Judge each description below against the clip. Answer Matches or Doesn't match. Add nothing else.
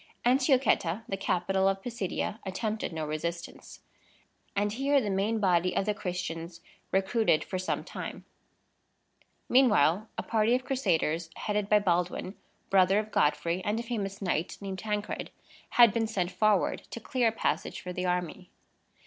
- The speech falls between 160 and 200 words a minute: Doesn't match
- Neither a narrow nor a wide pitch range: Matches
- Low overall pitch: Doesn't match